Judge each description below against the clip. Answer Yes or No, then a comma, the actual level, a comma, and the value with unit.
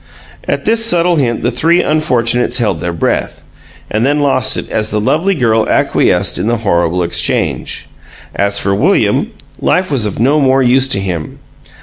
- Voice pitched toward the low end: Yes, low, 120 Hz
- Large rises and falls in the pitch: Yes, wide, 6.3 semitones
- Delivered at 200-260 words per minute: No, average, 175 wpm